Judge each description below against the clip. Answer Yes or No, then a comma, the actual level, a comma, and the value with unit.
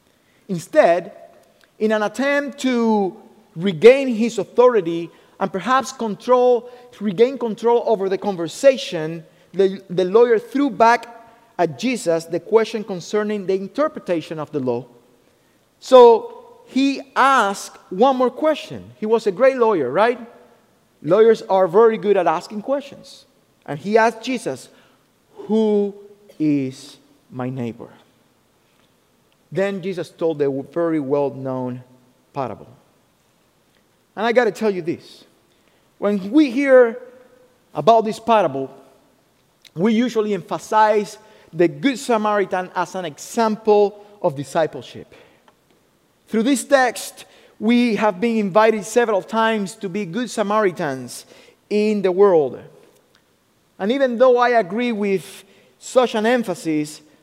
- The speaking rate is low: Yes, slow, 120 wpm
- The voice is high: Yes, high, 215 Hz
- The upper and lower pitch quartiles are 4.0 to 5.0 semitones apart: Yes, average, 4.7 semitones